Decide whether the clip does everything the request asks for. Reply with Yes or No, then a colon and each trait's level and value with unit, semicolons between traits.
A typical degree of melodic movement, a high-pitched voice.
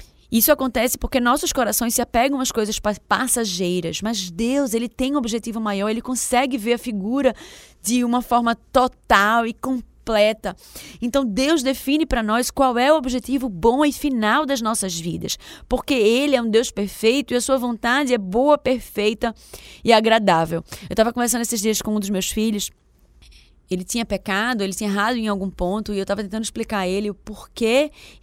Yes: average, 3.5 semitones; high, 230 Hz